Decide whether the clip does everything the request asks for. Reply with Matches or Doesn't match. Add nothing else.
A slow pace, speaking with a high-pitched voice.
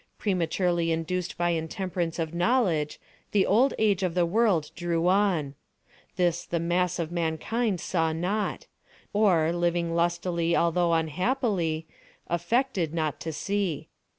Doesn't match